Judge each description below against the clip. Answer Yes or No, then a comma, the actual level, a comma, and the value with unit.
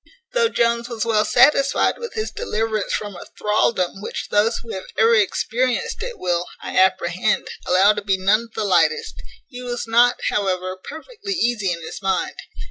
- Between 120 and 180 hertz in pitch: No, high, 215 Hz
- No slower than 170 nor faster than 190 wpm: Yes, average, 175 wpm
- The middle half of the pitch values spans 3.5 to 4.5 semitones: Yes, average, 4.2 semitones